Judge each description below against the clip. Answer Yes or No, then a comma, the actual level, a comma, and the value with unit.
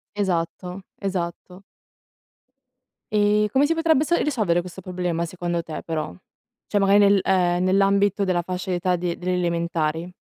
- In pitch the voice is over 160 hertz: Yes, medium, 185 Hz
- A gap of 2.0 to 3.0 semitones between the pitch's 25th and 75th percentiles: Yes, narrow, 2.5 semitones